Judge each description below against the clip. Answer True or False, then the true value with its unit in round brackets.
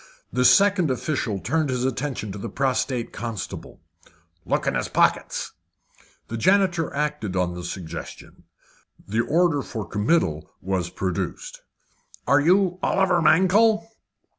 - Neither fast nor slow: False (125 wpm)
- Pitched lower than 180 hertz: True (140 Hz)